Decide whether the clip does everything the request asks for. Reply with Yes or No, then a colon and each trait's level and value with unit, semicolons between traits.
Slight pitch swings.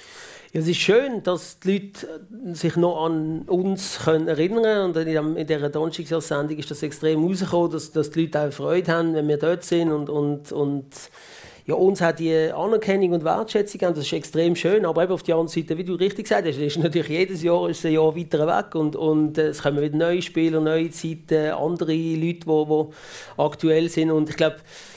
Yes: narrow, 2.0 semitones